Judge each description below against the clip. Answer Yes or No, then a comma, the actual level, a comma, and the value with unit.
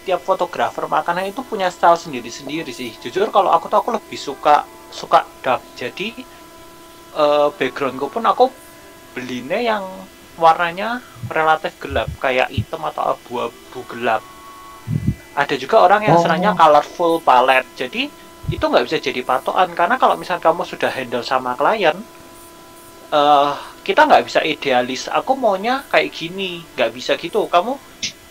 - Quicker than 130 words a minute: Yes, fast, 140 wpm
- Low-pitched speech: No, medium, 175 Hz